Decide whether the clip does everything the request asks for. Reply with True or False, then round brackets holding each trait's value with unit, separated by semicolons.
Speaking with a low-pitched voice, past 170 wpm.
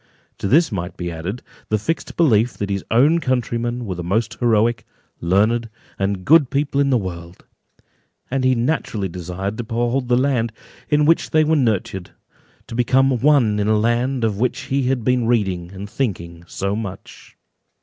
True (115 Hz; 180 wpm)